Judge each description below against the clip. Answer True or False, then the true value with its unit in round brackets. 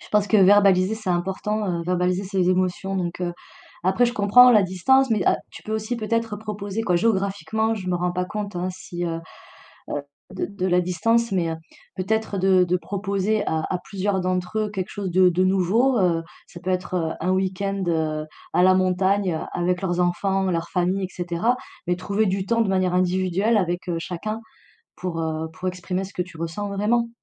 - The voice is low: False (185 Hz)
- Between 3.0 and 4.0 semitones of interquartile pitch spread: False (2.4 semitones)